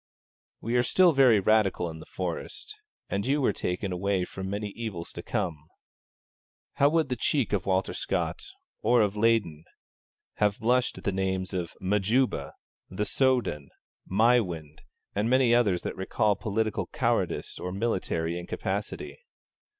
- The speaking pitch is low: Yes, low, 100 Hz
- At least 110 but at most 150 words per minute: Yes, average, 145 wpm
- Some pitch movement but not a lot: Yes, average, 4.3 semitones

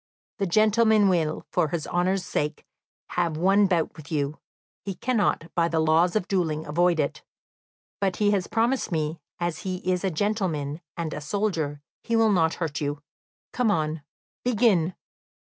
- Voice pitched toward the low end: No, medium, 175 Hz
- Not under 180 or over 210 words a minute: No, average, 165 wpm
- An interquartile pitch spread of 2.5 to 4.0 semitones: No, average, 4.4 semitones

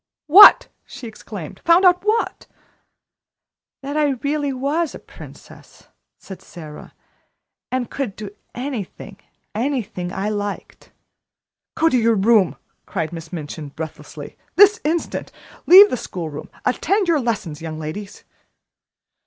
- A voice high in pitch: Yes, high, 230 Hz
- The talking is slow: Yes, slow, 130 wpm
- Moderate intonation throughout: No, wide, 8.9 semitones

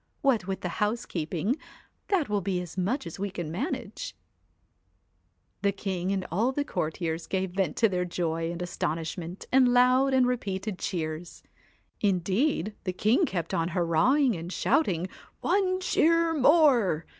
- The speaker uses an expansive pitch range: Yes, wide, 6.6 semitones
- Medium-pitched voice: No, high, 195 Hz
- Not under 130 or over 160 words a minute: Yes, average, 145 wpm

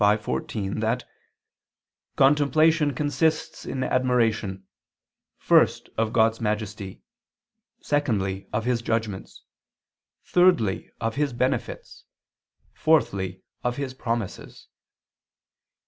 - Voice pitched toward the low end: Yes, low, 115 Hz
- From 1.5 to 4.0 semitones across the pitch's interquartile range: No, average, 4.8 semitones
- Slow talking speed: Yes, slow, 85 wpm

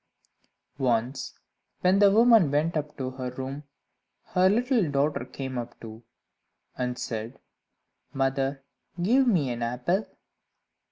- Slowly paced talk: Yes, slow, 120 wpm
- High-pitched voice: No, medium, 140 Hz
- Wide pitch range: Yes, wide, 6.4 semitones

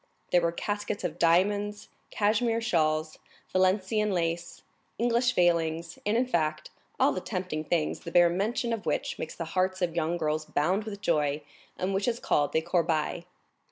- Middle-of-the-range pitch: Yes, medium, 175 Hz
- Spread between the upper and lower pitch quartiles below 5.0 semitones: Yes, average, 4.2 semitones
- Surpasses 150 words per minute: Yes, average, 165 wpm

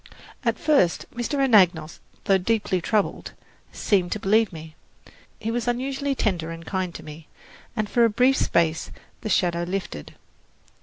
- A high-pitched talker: Yes, high, 200 Hz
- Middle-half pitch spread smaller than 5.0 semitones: No, wide, 5.6 semitones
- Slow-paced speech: No, average, 150 wpm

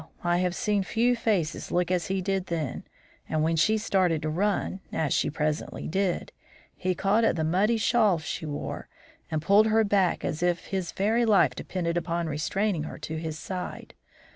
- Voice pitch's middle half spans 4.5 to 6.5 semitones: No, average, 3.9 semitones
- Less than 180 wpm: No, average, 185 wpm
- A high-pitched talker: No, medium, 180 Hz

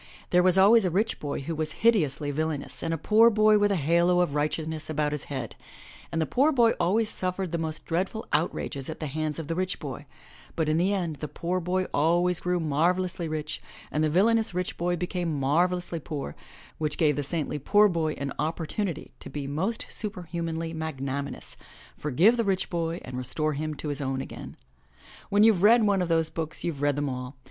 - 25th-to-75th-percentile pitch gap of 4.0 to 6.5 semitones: No, average, 3.5 semitones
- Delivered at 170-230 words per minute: Yes, fast, 205 wpm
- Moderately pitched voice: Yes, medium, 165 Hz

